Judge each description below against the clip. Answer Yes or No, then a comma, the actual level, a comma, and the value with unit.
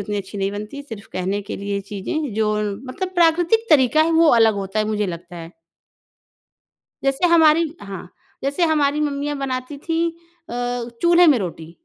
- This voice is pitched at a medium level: No, very high, 265 Hz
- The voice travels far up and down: Yes, wide, 7.7 semitones